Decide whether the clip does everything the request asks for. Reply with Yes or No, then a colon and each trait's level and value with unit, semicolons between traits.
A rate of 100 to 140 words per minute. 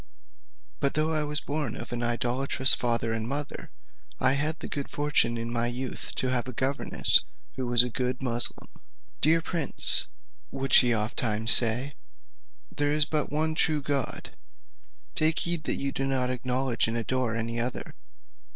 No: average, 165 wpm